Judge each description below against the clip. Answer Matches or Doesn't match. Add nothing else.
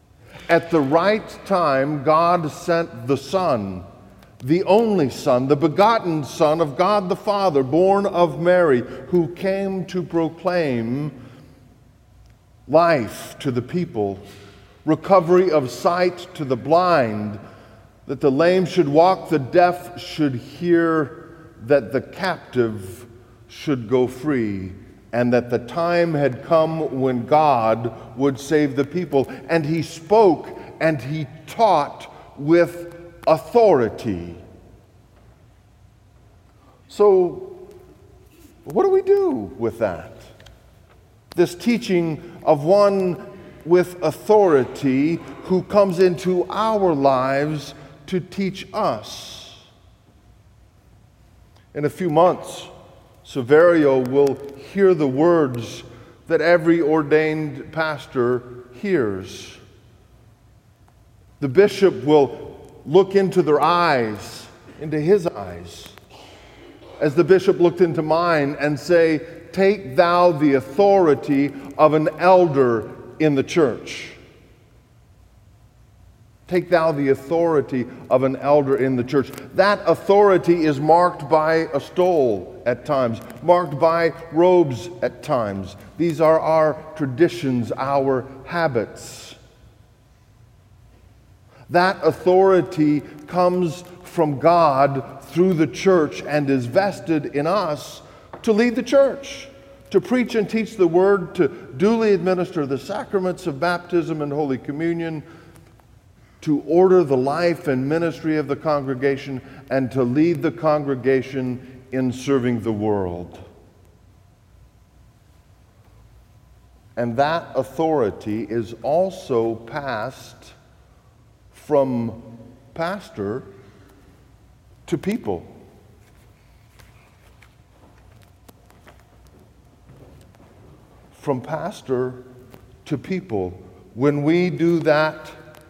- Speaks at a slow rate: Matches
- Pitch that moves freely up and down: Matches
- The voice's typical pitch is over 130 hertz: Matches